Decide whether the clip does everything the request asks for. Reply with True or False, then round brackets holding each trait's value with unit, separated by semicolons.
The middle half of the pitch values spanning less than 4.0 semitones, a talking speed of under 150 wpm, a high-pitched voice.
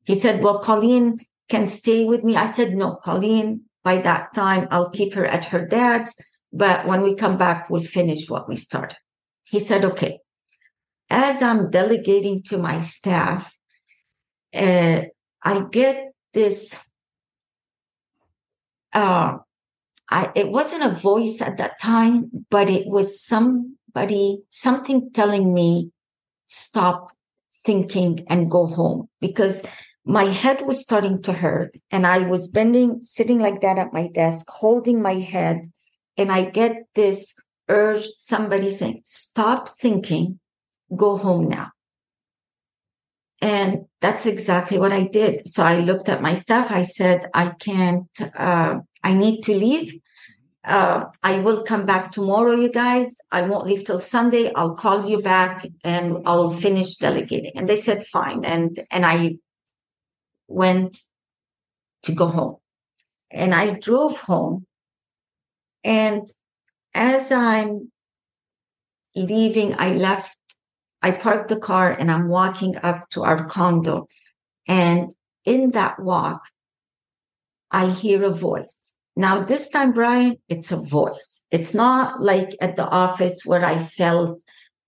True (3.5 semitones; 140 wpm; 195 Hz)